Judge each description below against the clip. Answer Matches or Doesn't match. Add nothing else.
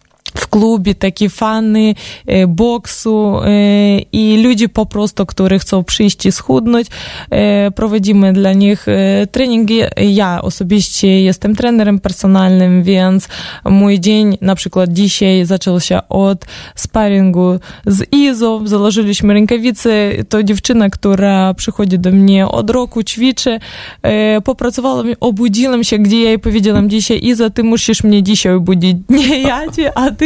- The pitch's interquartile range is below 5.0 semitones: Matches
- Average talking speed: Matches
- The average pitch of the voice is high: Matches